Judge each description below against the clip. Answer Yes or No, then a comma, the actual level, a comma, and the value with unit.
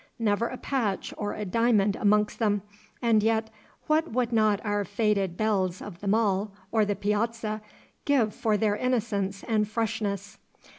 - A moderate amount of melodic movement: No, narrow, 1.9 semitones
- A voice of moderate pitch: No, high, 215 Hz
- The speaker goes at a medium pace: Yes, average, 155 wpm